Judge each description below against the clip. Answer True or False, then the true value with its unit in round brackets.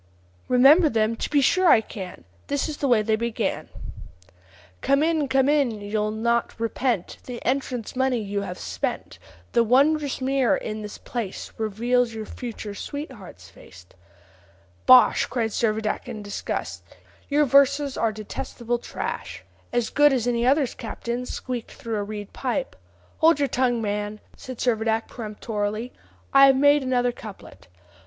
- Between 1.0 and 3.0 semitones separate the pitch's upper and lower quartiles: False (3.8 semitones)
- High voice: True (235 Hz)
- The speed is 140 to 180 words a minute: True (150 wpm)